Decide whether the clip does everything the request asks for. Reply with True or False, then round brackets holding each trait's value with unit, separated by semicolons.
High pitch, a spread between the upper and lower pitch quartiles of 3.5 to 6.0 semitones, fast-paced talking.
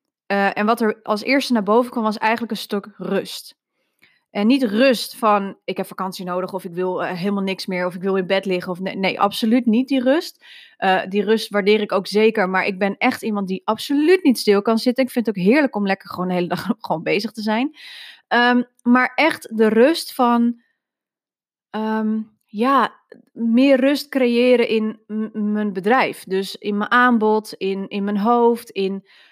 True (220 Hz; 3.9 semitones; 205 wpm)